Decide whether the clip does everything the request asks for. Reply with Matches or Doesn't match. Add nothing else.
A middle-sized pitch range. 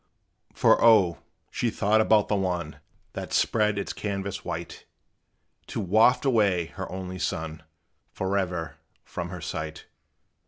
Matches